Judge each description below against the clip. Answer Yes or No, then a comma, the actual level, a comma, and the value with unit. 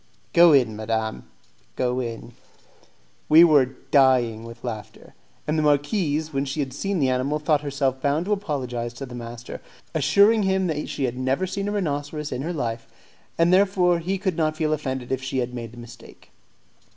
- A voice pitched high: No, medium, 140 Hz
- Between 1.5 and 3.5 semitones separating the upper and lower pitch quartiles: No, average, 4.7 semitones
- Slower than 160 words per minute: No, average, 185 wpm